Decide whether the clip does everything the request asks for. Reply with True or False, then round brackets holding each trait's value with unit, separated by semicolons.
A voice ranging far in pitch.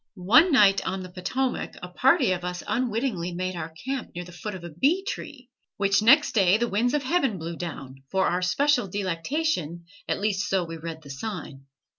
True (6.4 semitones)